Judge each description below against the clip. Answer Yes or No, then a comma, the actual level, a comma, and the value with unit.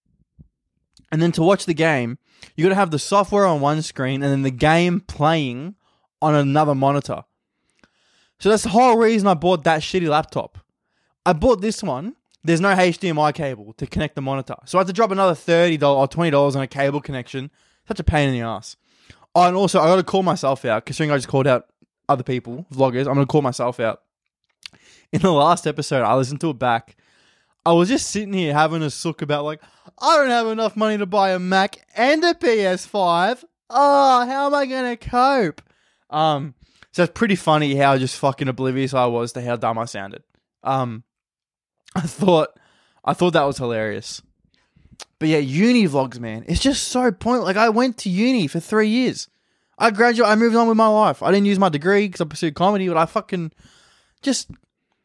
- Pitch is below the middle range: No, medium, 165 Hz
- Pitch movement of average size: No, wide, 6.6 semitones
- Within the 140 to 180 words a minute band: No, average, 200 wpm